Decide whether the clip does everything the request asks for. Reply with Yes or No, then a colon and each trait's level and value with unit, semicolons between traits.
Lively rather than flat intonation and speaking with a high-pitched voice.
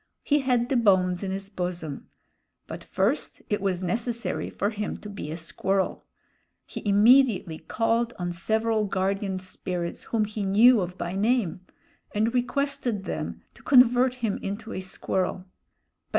No: average, 4.0 semitones; high, 205 Hz